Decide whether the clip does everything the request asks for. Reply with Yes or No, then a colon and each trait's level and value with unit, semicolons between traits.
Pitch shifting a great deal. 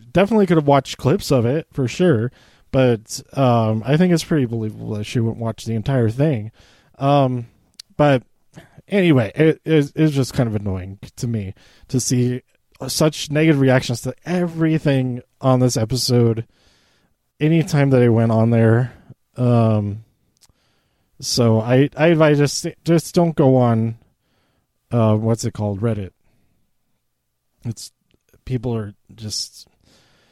No: average, 4.6 semitones